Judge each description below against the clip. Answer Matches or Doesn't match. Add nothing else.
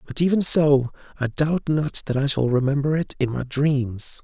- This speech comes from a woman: Doesn't match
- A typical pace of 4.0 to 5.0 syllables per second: Matches